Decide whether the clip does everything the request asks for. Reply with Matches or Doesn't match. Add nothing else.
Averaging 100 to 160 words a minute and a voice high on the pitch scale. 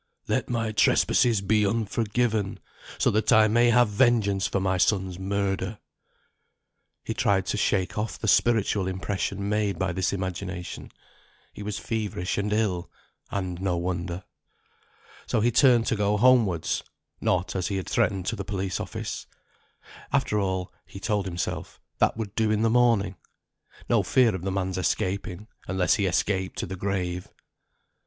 Doesn't match